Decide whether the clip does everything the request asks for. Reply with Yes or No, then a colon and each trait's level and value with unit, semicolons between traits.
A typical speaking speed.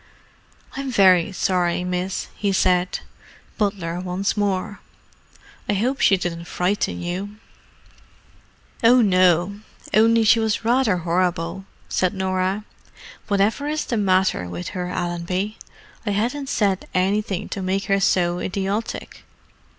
No: slow, 115 wpm